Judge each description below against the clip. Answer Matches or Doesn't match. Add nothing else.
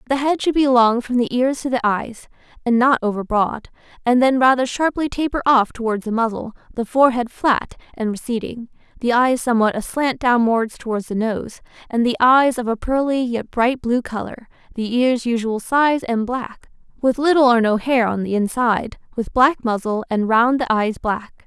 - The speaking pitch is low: Doesn't match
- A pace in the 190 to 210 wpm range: Matches